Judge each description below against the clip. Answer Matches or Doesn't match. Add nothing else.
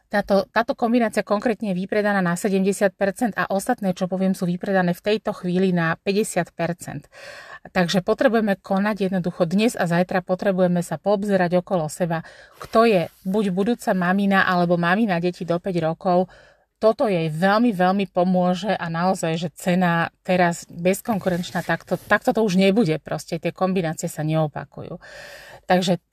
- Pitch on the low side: Doesn't match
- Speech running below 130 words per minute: Doesn't match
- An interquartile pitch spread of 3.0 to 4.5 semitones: Doesn't match